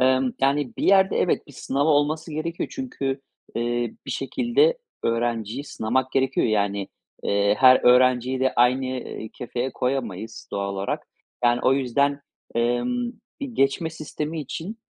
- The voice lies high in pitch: No, low, 130 Hz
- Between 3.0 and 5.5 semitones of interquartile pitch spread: Yes, average, 3.8 semitones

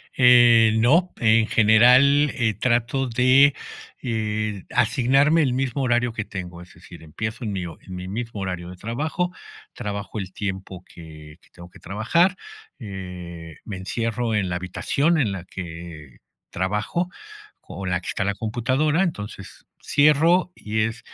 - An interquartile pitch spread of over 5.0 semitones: Yes, wide, 5.4 semitones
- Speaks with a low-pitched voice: Yes, low, 110 Hz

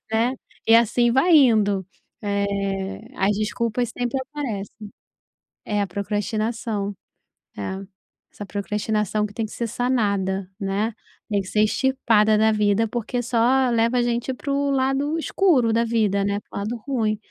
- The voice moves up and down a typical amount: Yes, average, 3.2 semitones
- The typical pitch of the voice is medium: No, high, 220 Hz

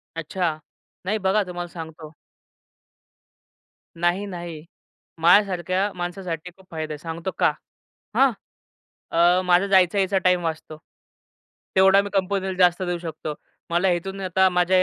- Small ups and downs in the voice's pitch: Yes, narrow, 2.3 semitones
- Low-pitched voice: No, medium, 180 Hz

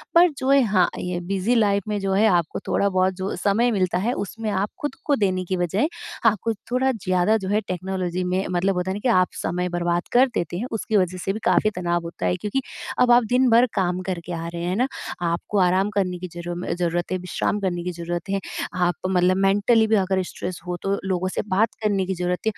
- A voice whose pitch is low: No, high, 190 Hz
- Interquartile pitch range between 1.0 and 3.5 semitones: Yes, average, 2.9 semitones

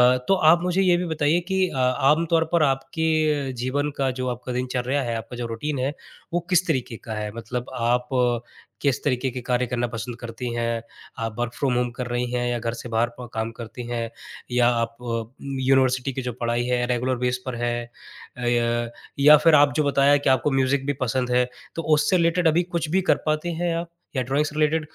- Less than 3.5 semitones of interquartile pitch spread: No, average, 3.8 semitones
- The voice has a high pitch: No, low, 130 Hz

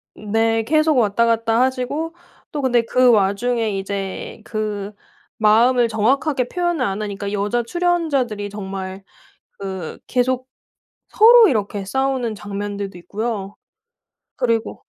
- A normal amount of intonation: Yes, average, 4.1 semitones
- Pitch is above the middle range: Yes, high, 225 Hz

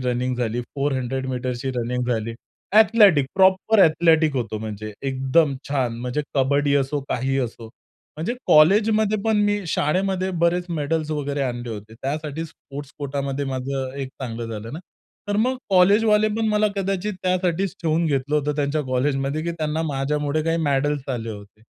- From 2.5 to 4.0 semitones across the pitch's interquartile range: No, average, 4.8 semitones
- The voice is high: No, medium, 145 Hz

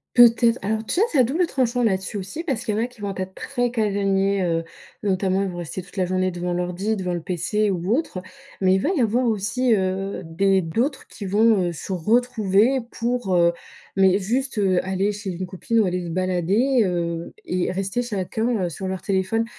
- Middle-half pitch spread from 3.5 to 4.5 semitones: Yes, average, 3.8 semitones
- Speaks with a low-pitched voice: No, high, 195 Hz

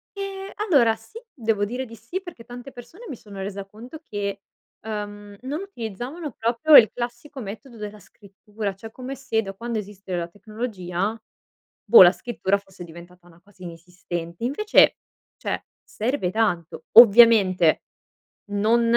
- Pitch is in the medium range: No, high, 220 Hz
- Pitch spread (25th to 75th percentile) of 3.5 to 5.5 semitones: Yes, average, 3.9 semitones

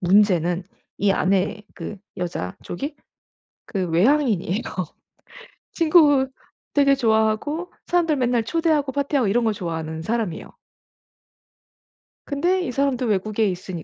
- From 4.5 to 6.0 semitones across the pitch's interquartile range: No, wide, 7.2 semitones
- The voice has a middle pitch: No, high, 225 Hz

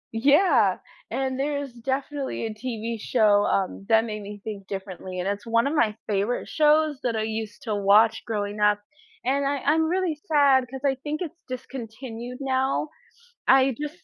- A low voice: No, high, 245 Hz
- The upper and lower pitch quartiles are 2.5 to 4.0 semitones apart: No, average, 4.7 semitones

